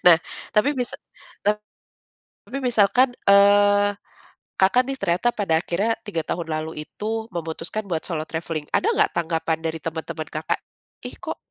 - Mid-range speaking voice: Yes, medium, 175 Hz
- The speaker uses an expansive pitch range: No, average, 4.1 semitones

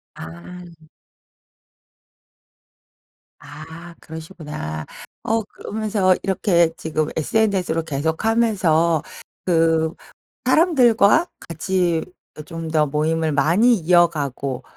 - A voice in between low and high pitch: Yes, medium, 165 Hz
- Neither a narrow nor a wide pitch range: Yes, average, 3.6 semitones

